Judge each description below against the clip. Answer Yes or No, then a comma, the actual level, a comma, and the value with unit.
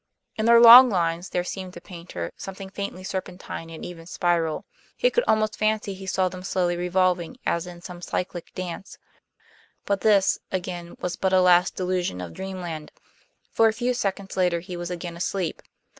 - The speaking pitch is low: No, medium, 185 Hz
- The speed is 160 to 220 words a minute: Yes, average, 175 wpm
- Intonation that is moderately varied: No, narrow, 2.0 semitones